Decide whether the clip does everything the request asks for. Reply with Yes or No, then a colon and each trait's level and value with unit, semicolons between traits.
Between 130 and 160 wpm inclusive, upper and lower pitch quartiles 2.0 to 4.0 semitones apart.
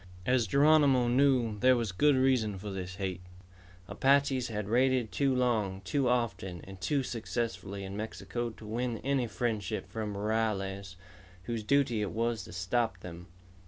No: average, 155 wpm; average, 4.4 semitones